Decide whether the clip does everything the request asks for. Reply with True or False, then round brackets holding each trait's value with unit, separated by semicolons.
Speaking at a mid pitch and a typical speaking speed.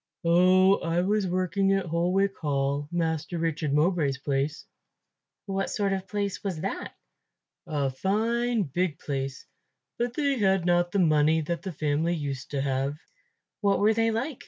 True (175 Hz; 160 wpm)